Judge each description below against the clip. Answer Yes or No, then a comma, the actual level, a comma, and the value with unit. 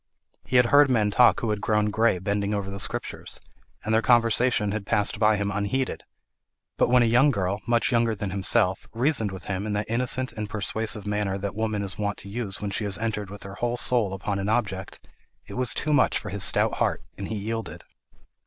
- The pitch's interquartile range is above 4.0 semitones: No, narrow, 2.6 semitones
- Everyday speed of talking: No, fast, 220 wpm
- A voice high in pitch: No, low, 105 Hz